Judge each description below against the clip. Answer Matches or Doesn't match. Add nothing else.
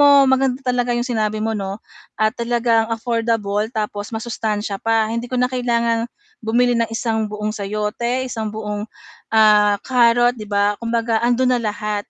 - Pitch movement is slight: Matches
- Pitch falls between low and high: Doesn't match